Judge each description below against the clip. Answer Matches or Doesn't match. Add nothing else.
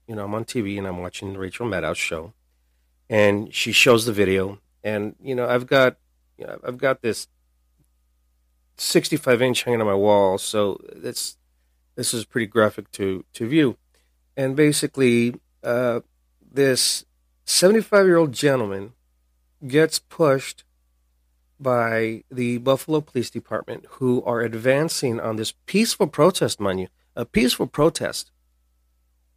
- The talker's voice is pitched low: Matches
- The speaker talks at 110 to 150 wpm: Matches